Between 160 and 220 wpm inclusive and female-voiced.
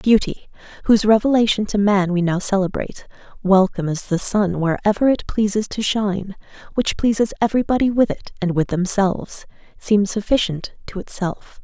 No: average, 150 wpm; female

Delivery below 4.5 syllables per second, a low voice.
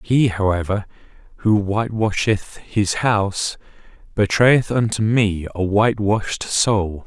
Yes: 4.0 syllables/s; low, 105 Hz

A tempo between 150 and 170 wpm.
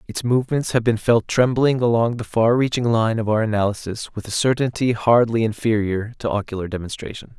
No: average, 180 wpm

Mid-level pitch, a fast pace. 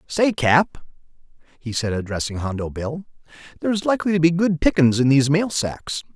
No: medium, 150 Hz; average, 165 wpm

